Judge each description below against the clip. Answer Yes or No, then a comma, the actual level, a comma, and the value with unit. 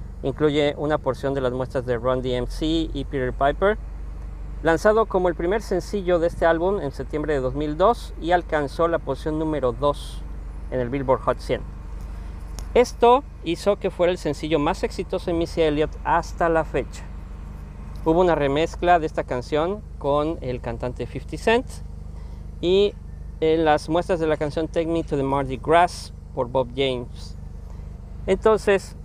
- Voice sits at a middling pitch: Yes, medium, 150 Hz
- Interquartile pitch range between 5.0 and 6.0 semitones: Yes, wide, 5.5 semitones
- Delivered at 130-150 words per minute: No, average, 160 wpm